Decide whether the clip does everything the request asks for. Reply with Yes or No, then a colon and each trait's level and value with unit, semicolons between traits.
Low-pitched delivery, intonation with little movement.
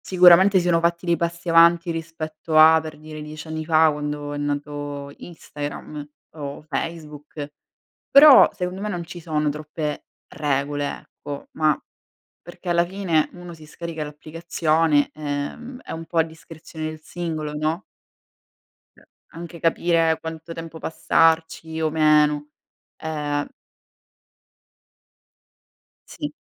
No: medium, 160 Hz; narrow, 2.1 semitones